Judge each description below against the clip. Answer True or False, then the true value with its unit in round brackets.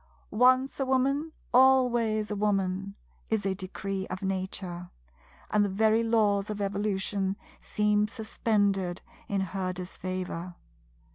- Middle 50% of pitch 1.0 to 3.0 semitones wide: True (2.7 semitones)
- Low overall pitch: False (200 Hz)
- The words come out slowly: True (120 wpm)